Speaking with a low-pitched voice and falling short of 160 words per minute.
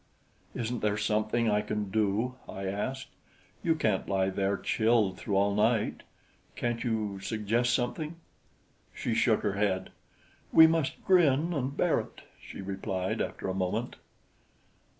Yes: low, 110 Hz; average, 140 wpm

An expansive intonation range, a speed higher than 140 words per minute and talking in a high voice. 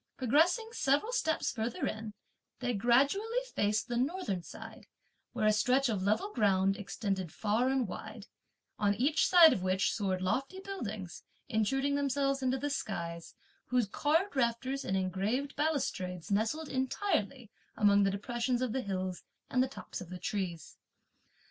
Yes: wide, 5.7 semitones; average, 150 wpm; high, 235 Hz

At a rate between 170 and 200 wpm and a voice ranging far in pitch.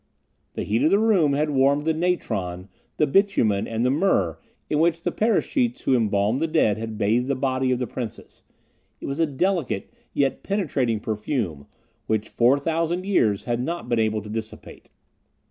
Yes: average, 180 wpm; wide, 6.9 semitones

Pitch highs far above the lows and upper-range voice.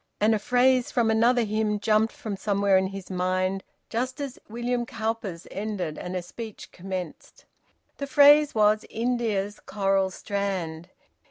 No: average, 3.7 semitones; high, 215 Hz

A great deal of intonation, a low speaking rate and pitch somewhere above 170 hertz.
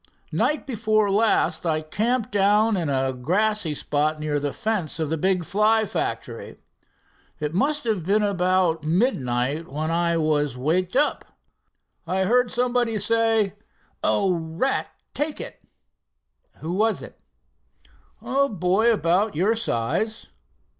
Yes: wide, 5.8 semitones; slow, 130 wpm; high, 190 Hz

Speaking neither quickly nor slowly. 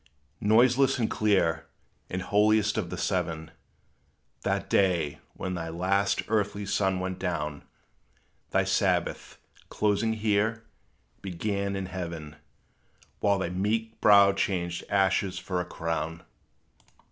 No: slow, 115 wpm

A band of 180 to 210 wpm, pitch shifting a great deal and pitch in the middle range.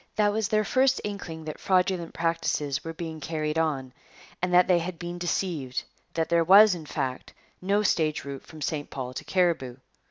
No: average, 185 wpm; average, 3.3 semitones; medium, 165 Hz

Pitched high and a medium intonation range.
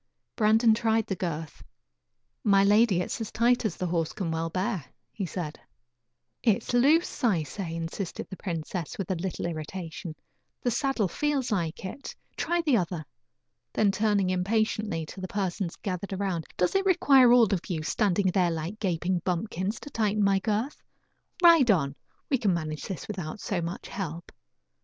Yes: high, 195 Hz; average, 4.4 semitones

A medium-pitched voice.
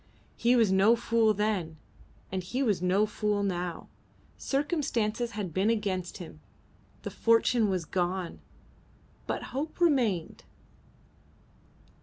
No: high, 210 Hz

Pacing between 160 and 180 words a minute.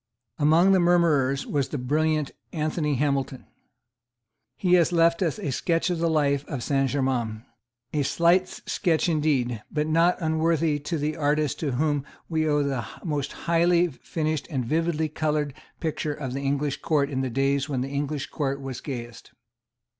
Yes: average, 165 wpm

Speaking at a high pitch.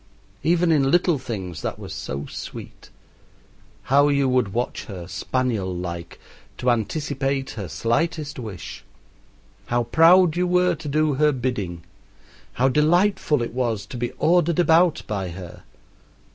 No: low, 130 Hz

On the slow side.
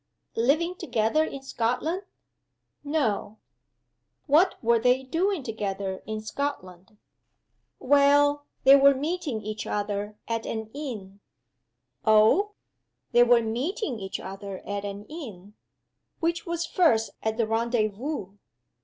Yes: slow, 115 wpm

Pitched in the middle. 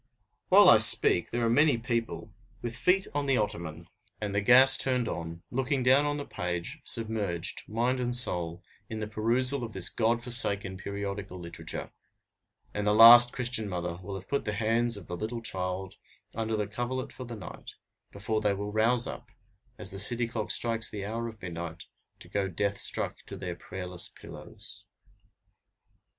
No: low, 110 Hz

